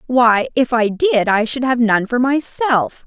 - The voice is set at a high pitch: Yes, very high, 250 Hz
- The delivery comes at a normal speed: Yes, average, 195 wpm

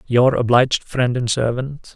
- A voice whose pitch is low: Yes, low, 125 Hz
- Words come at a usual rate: Yes, average, 155 wpm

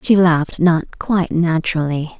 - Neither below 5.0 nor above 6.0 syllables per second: No, 4.8 syllables/s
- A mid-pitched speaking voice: Yes, medium, 165 Hz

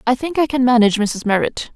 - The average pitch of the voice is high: Yes, high, 245 Hz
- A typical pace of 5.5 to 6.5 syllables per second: Yes, 6.4 syllables/s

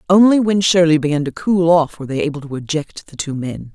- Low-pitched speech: No, medium, 160 Hz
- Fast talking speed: Yes, fast, 240 wpm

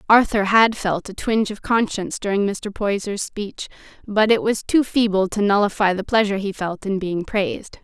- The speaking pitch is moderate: No, high, 205 Hz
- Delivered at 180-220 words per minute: Yes, average, 190 wpm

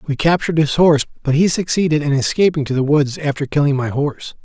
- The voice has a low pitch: No, medium, 150 Hz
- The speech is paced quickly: Yes, fast, 215 wpm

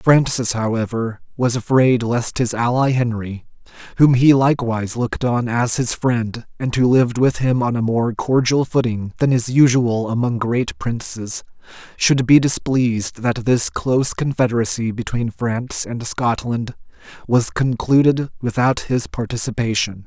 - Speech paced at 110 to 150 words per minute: Yes, average, 145 wpm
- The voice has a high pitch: No, low, 120 Hz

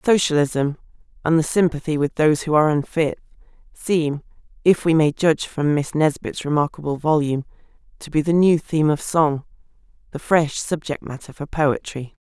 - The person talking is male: No, female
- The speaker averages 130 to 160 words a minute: Yes, average, 155 wpm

